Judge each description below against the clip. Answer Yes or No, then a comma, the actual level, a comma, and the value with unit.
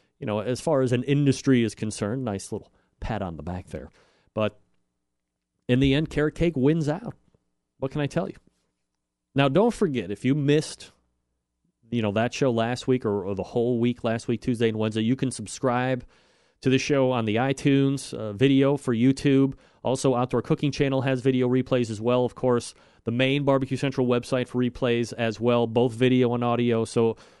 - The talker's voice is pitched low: Yes, low, 125 Hz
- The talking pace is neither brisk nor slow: Yes, average, 195 wpm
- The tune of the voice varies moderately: Yes, average, 3.7 semitones